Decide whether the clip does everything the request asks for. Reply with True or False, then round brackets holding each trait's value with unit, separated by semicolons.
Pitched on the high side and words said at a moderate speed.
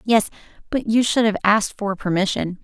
True (210 Hz; 180 wpm)